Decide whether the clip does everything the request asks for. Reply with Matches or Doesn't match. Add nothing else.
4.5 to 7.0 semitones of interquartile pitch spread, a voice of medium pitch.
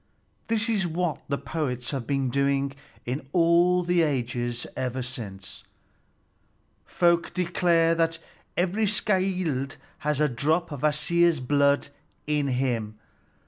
Matches